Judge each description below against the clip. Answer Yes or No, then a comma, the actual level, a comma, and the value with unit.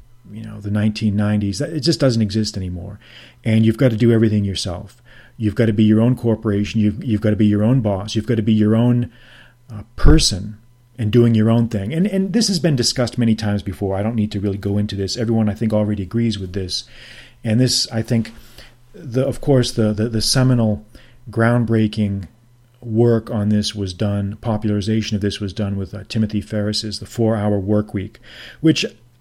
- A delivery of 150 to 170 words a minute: No, fast, 205 wpm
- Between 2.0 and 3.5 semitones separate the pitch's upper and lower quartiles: Yes, narrow, 2.4 semitones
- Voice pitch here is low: Yes, low, 110 Hz